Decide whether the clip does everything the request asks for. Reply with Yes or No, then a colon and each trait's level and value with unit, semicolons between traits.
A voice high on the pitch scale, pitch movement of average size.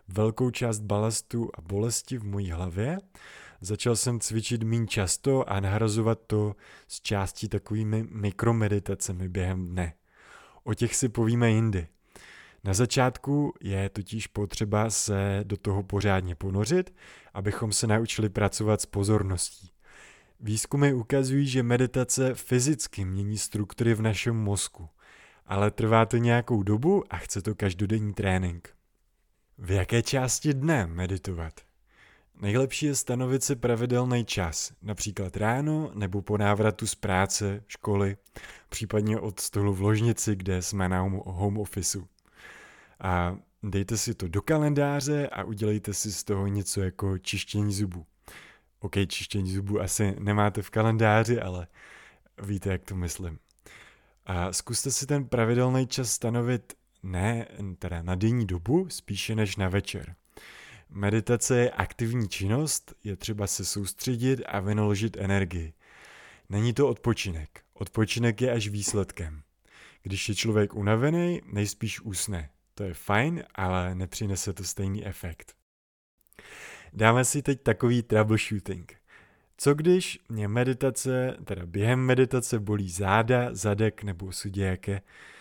No: low, 105 Hz; average, 3.2 semitones